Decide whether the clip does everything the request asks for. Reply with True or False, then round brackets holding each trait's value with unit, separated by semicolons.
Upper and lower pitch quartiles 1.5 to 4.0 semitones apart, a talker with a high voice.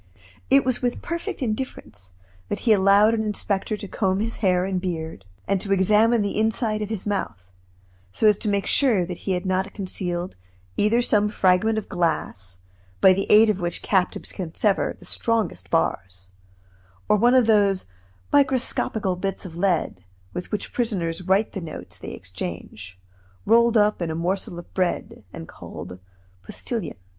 True (3.7 semitones; 195 Hz)